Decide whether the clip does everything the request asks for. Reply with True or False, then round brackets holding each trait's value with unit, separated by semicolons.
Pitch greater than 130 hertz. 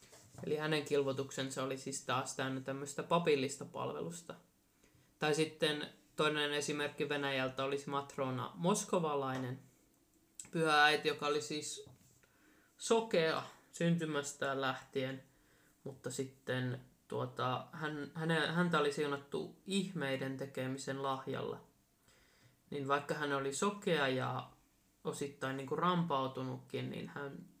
True (140 Hz)